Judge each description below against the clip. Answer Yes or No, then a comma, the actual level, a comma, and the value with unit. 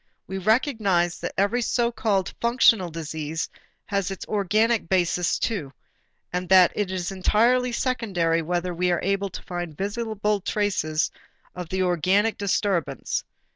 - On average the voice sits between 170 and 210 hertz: Yes, high, 190 Hz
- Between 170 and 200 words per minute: No, slow, 135 wpm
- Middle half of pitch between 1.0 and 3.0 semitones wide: No, average, 3.5 semitones